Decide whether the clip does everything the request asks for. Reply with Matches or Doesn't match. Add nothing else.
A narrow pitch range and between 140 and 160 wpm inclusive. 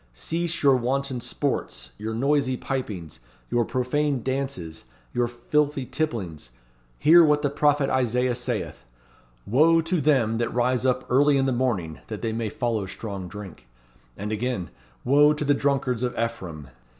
Doesn't match